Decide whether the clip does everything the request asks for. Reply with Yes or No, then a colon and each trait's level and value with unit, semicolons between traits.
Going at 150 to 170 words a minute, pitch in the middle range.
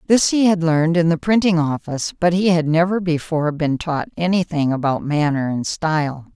No: average, 200 wpm; medium, 165 Hz